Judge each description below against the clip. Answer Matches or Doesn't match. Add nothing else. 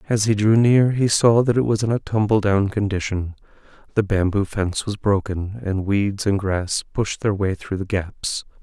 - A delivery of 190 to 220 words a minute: Matches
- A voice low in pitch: Matches